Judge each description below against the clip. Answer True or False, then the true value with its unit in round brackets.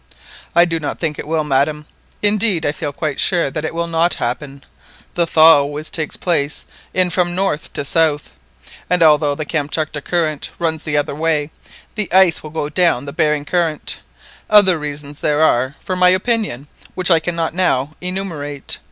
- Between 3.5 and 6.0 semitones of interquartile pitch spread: False (3.0 semitones)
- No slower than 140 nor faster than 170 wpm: False (180 wpm)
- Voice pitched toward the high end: False (160 Hz)